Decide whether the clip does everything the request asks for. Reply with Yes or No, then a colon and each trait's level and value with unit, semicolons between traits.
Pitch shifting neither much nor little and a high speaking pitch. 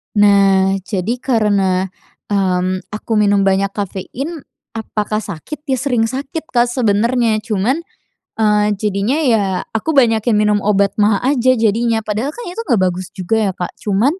Yes: average, 3.3 semitones; high, 215 Hz